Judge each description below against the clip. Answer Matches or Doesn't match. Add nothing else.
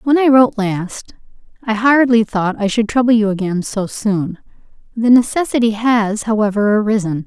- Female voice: Matches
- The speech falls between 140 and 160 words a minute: Matches